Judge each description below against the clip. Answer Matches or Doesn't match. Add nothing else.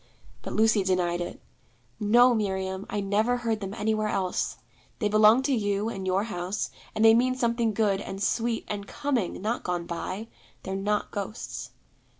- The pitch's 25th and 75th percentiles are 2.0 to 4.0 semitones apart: Matches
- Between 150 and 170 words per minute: Matches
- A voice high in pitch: Matches